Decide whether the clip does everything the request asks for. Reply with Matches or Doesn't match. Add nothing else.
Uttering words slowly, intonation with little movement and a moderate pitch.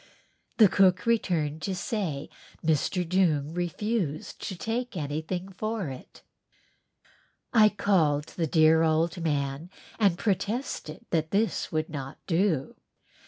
Doesn't match